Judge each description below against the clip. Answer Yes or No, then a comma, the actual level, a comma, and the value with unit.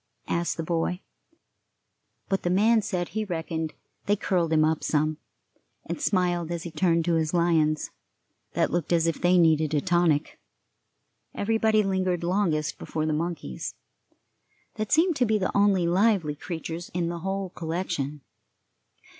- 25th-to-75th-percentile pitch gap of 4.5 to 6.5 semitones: No, average, 3.1 semitones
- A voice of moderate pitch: Yes, medium, 175 Hz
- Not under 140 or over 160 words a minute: Yes, average, 150 wpm